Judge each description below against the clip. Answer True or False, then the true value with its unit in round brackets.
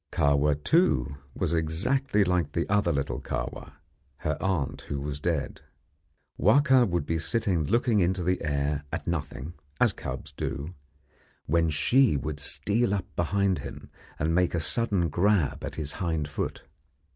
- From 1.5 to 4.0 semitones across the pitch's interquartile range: False (5.2 semitones)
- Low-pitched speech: True (85 Hz)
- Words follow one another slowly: False (150 wpm)